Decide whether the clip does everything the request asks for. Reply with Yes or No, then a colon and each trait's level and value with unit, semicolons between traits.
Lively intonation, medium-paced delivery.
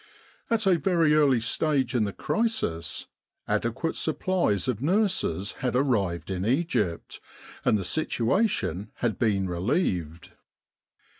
No: wide, 8.9 semitones; slow, 120 wpm